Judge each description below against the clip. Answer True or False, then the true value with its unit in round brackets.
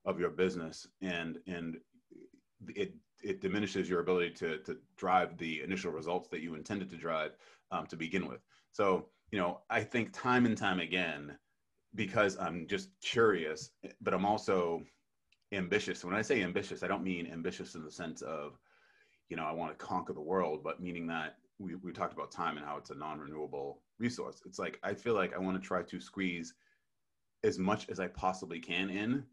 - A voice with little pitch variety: False (3.7 semitones)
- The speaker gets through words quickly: False (190 wpm)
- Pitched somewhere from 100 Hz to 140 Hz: False (90 Hz)